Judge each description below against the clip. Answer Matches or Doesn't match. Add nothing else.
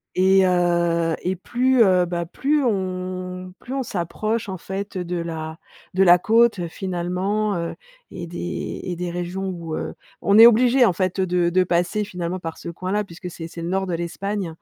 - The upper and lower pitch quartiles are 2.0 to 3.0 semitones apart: Matches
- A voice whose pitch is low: Doesn't match